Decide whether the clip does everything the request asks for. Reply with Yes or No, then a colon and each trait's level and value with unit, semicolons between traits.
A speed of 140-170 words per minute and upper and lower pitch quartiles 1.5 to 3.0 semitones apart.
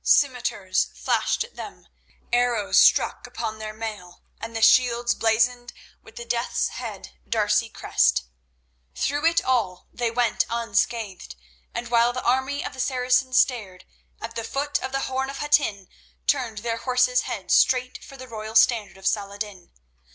Yes: average, 155 wpm; average, 2.7 semitones